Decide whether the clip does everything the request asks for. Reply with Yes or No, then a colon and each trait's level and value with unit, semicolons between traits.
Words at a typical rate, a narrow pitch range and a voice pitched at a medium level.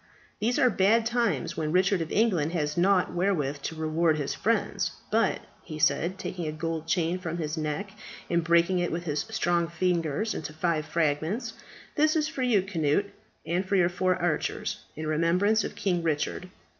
No: average, 180 wpm; average, 3.6 semitones; medium, 170 Hz